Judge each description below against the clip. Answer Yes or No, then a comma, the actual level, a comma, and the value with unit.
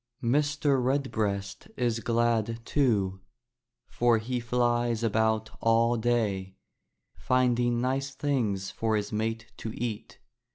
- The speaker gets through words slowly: Yes, slow, 110 wpm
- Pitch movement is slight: Yes, narrow, 2.2 semitones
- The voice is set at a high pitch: No, low, 115 Hz